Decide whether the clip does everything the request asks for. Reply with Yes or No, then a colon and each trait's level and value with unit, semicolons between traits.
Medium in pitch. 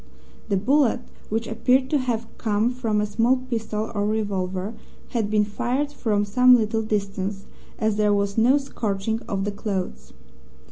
No: high, 215 Hz